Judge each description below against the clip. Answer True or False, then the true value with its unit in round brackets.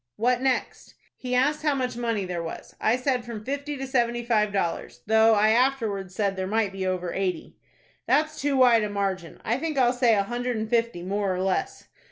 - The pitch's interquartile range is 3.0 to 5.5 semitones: True (4.2 semitones)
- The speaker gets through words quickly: True (210 wpm)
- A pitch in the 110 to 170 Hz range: False (225 Hz)